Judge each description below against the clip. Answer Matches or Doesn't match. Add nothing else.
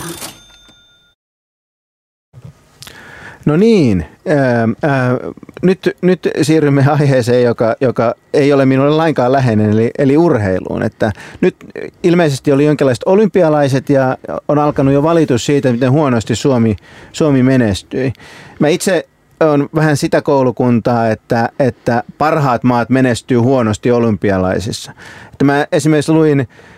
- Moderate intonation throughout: Matches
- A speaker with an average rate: Matches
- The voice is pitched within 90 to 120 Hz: Doesn't match